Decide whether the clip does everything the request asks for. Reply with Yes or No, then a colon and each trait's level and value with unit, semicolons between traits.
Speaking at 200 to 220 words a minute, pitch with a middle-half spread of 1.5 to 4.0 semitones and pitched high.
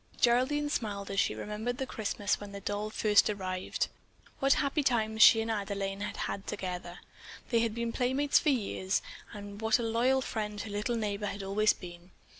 No: average, 190 wpm; average, 2.8 semitones; high, 215 Hz